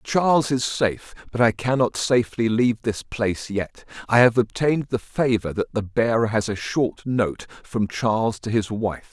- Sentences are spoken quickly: No, average, 185 wpm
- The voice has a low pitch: Yes, low, 115 Hz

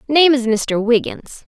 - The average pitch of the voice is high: Yes, very high, 250 Hz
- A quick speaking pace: No, average, 155 wpm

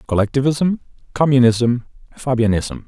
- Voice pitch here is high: No, low, 125 Hz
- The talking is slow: Yes, slow, 65 wpm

